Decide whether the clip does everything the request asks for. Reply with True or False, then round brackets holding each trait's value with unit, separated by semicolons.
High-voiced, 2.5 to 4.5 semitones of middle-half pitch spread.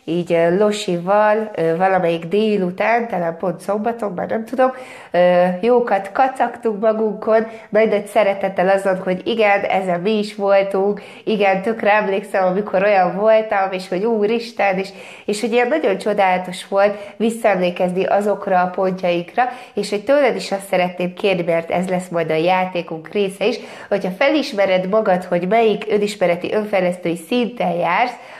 True (200 Hz; 2.9 semitones)